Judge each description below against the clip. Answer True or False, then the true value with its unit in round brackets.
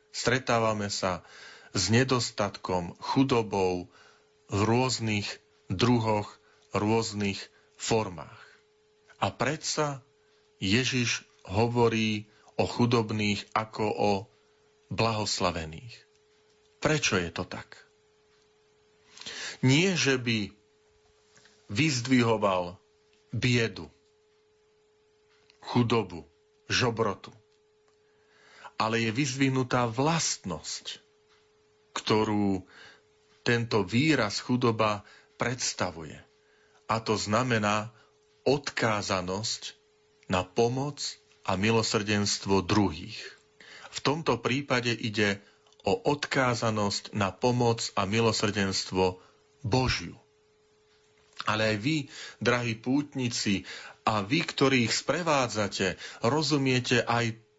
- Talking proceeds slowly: True (75 wpm)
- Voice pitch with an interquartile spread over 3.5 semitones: True (5.0 semitones)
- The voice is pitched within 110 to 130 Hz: True (115 Hz)